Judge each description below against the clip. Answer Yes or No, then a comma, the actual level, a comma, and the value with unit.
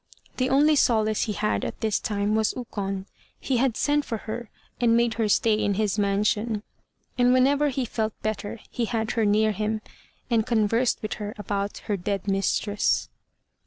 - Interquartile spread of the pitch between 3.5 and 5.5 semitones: No, narrow, 2.5 semitones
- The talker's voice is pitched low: No, high, 220 Hz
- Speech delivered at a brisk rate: No, average, 175 wpm